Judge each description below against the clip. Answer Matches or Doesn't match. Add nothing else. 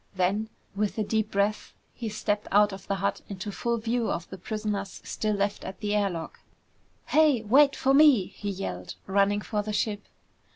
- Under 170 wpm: Doesn't match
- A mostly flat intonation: Matches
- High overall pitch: Matches